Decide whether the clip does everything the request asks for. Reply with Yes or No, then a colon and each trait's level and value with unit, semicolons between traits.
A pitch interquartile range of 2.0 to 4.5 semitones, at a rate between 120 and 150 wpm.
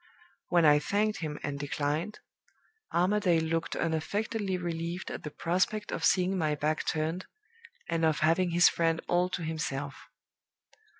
Yes: average, 2.8 semitones; average, 140 wpm